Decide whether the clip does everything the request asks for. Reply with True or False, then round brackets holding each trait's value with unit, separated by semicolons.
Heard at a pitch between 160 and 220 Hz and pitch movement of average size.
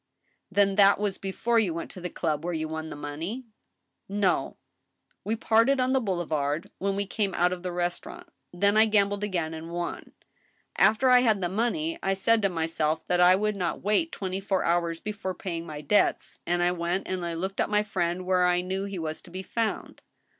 True (190 Hz; 3.2 semitones)